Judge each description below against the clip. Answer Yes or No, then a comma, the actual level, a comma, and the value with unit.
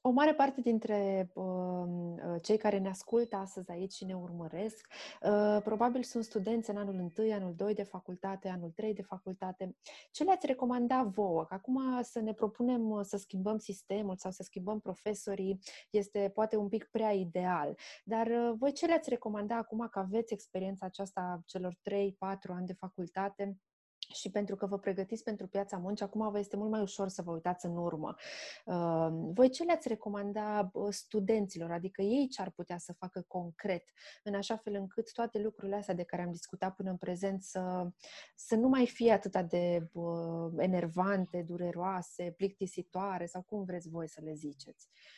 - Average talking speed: No, fast, 175 wpm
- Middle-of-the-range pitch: No, high, 200 Hz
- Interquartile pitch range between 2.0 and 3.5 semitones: Yes, average, 3.1 semitones